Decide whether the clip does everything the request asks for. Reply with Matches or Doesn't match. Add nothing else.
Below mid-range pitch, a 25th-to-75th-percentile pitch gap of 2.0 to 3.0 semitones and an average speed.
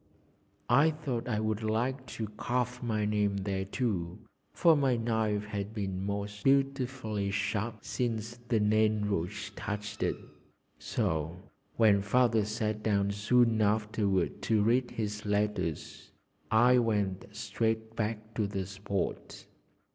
Doesn't match